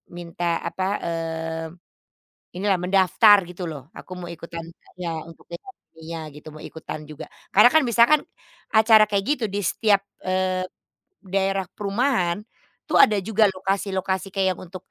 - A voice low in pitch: No, medium, 185 Hz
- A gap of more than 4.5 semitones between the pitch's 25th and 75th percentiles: No, average, 3.3 semitones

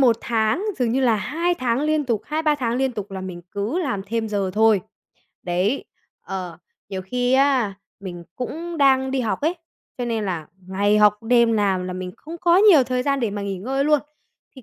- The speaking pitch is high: Yes, high, 235 Hz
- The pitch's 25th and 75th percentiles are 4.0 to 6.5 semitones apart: Yes, average, 5.2 semitones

